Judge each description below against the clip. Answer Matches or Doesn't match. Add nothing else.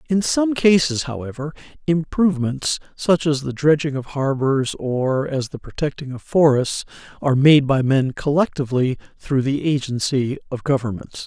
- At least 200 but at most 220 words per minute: Doesn't match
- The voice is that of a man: Matches